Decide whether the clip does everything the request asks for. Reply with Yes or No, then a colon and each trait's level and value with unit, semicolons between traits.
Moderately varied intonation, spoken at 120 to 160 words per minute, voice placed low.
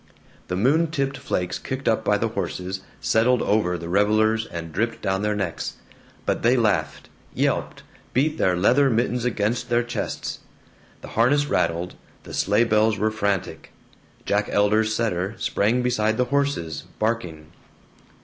Yes: average, 4.1 semitones; average, 150 wpm; low, 110 Hz